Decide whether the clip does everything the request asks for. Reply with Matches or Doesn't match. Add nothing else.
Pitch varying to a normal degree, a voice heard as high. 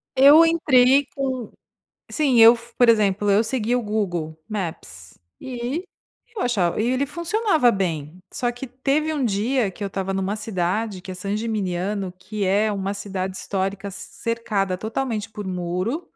Matches